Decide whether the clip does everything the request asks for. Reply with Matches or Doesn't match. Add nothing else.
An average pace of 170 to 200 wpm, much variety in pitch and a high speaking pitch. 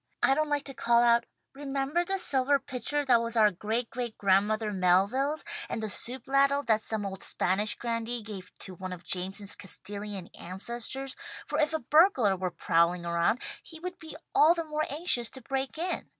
Matches